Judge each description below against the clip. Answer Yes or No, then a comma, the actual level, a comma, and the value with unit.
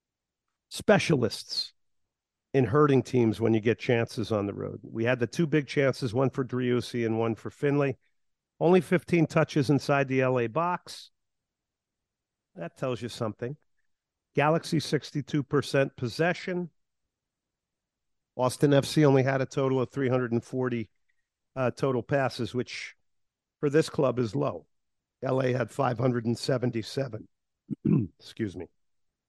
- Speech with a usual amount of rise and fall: Yes, average, 3.7 semitones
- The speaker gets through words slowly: Yes, slow, 125 wpm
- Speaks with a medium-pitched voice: No, low, 130 Hz